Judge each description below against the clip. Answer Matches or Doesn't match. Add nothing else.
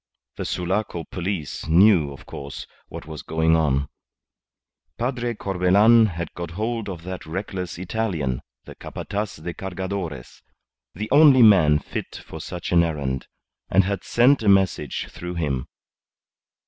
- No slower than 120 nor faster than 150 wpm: Matches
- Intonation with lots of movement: Doesn't match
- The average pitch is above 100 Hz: Doesn't match